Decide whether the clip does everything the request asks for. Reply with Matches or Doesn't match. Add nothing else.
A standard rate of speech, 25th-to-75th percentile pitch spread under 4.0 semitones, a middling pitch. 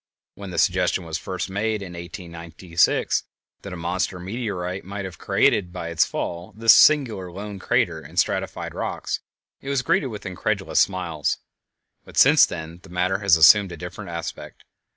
Doesn't match